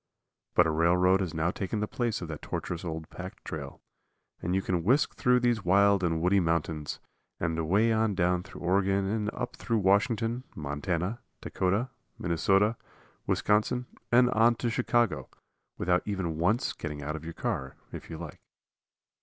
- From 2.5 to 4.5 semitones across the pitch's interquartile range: No, average, 4.9 semitones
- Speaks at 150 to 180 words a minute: Yes, average, 160 wpm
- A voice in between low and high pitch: No, very low, 95 Hz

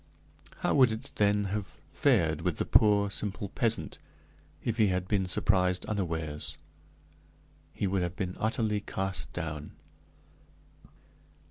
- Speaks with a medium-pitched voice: No, low, 100 Hz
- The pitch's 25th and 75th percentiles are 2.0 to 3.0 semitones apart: Yes, average, 2.7 semitones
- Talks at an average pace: No, slow, 125 wpm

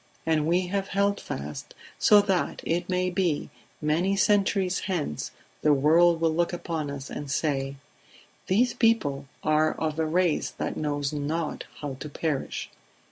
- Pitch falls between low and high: Yes, medium, 160 Hz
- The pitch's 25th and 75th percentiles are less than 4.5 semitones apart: Yes, average, 3.8 semitones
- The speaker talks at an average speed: Yes, average, 150 wpm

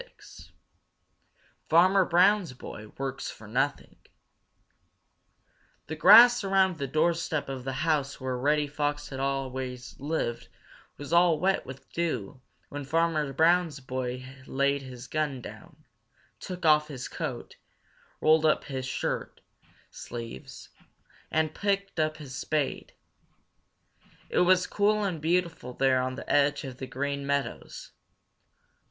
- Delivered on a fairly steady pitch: No, average, 4.1 semitones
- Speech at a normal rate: No, slow, 125 wpm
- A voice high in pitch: No, medium, 145 Hz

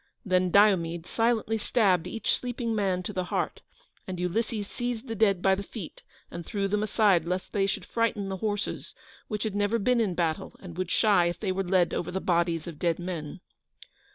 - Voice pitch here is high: Yes, high, 195 Hz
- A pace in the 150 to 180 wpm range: No, average, 200 wpm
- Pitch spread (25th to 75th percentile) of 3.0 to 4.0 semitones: Yes, average, 3.3 semitones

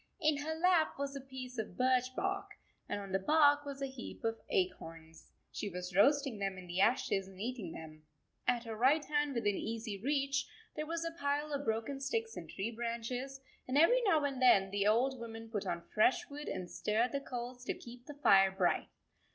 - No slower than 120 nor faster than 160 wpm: No, fast, 205 wpm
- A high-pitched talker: Yes, very high, 250 Hz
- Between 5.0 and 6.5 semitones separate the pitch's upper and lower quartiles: Yes, wide, 5.6 semitones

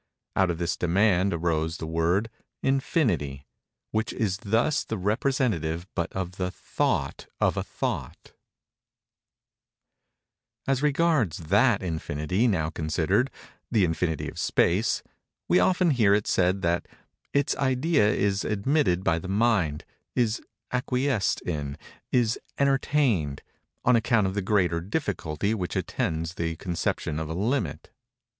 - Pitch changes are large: Yes, wide, 6.5 semitones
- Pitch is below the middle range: Yes, low, 100 Hz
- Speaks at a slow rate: Yes, slow, 120 wpm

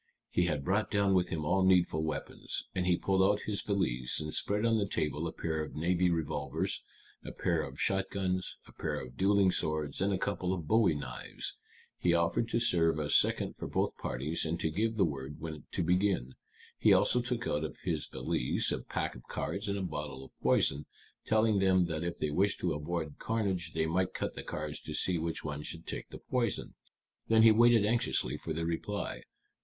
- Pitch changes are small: No, average, 4.4 semitones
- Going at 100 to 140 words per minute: No, fast, 205 wpm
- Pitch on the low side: Yes, very low, 90 Hz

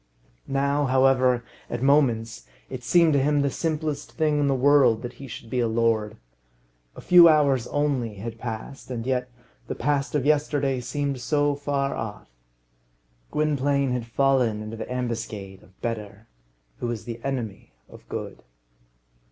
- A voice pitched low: Yes, low, 130 Hz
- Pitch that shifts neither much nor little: Yes, average, 3.8 semitones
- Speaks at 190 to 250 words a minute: No, average, 155 wpm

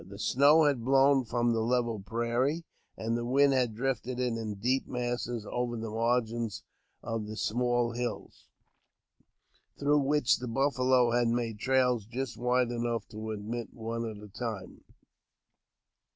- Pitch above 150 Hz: No, low, 120 Hz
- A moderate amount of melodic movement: No, narrow, 2.0 semitones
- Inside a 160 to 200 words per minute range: No, average, 150 wpm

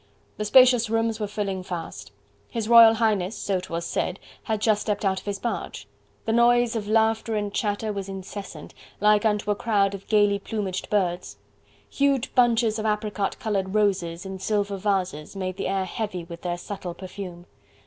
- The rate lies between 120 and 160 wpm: No, average, 175 wpm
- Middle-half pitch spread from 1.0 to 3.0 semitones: Yes, narrow, 2.6 semitones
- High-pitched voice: Yes, high, 205 Hz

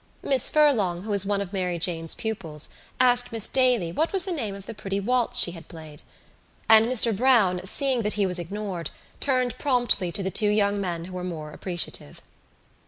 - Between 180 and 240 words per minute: Yes, average, 195 wpm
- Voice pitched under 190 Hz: No, high, 200 Hz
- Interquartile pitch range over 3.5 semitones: Yes, average, 5.3 semitones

